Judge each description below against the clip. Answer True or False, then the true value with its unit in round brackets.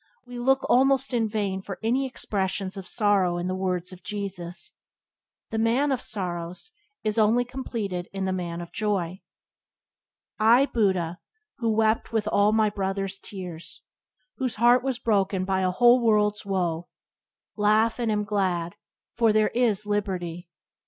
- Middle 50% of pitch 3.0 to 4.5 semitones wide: True (3.5 semitones)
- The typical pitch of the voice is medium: False (205 Hz)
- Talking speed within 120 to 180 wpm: True (150 wpm)